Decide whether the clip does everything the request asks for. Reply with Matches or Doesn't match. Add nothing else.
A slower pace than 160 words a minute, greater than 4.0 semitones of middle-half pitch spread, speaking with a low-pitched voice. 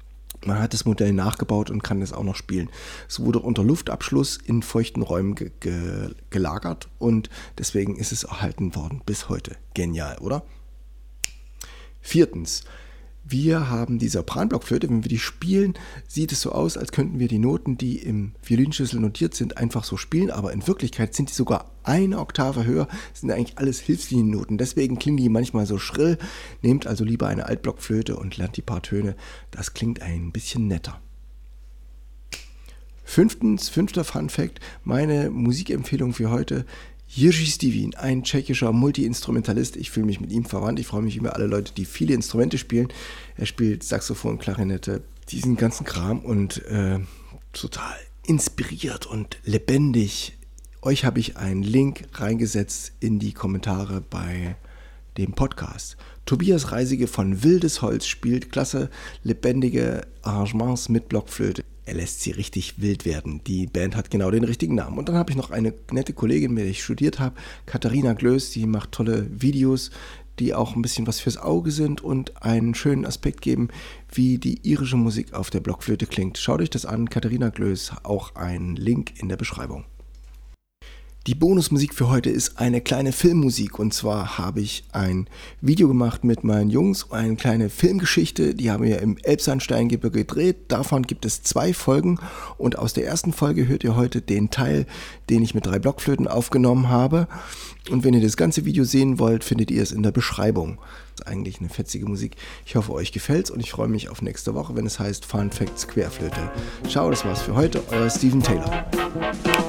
Doesn't match